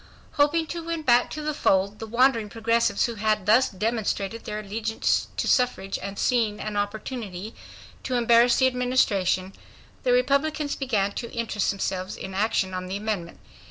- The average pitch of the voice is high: Yes, high, 225 Hz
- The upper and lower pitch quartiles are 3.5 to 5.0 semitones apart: Yes, average, 3.9 semitones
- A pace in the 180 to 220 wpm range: No, average, 160 wpm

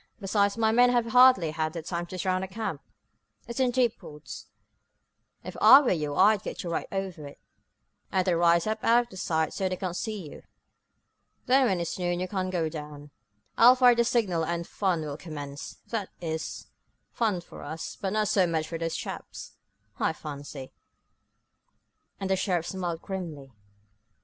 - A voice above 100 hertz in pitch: Yes, medium, 185 Hz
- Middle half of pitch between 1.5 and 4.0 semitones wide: No, average, 4.9 semitones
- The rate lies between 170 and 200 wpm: Yes, average, 180 wpm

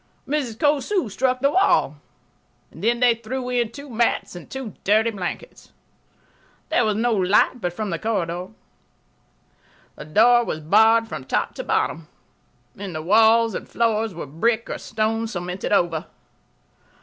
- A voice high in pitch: Yes, high, 220 Hz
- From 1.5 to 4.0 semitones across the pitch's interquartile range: No, average, 4.6 semitones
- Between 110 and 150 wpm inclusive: Yes, average, 145 wpm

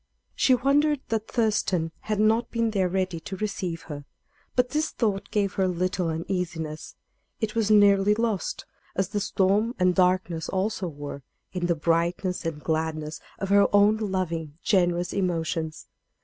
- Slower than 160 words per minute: Yes, average, 150 wpm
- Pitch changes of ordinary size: Yes, average, 4.0 semitones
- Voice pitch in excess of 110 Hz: Yes, medium, 185 Hz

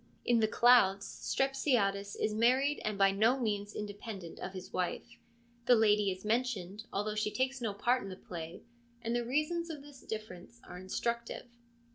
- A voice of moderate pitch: No, high, 215 Hz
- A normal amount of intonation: Yes, average, 3.9 semitones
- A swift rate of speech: No, average, 170 wpm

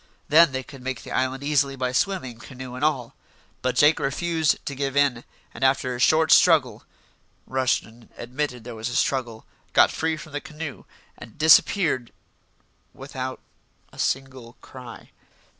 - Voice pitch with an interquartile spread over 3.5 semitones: No, average, 2.7 semitones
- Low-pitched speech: Yes, low, 130 Hz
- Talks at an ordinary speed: Yes, average, 155 wpm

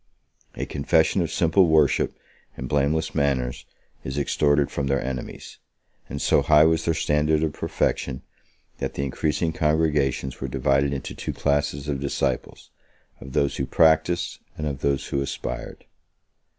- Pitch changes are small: Yes, narrow, 2.3 semitones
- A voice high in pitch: No, very low, 70 Hz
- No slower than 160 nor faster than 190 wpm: No, average, 150 wpm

